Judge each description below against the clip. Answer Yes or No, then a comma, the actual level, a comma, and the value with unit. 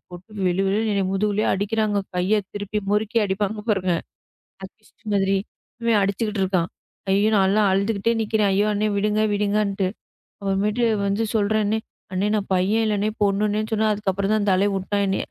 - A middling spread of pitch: No, narrow, 1.5 semitones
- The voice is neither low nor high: No, high, 205 Hz